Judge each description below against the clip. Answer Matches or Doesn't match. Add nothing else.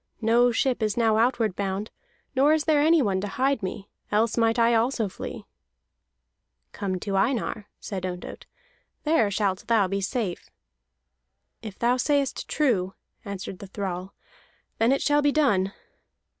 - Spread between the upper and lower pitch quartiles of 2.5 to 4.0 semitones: Doesn't match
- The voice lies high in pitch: Matches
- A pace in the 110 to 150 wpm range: Matches